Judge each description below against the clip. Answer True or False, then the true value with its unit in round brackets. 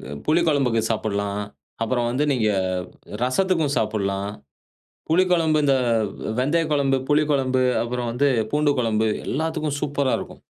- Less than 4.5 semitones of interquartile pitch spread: False (4.8 semitones)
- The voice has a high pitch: False (135 Hz)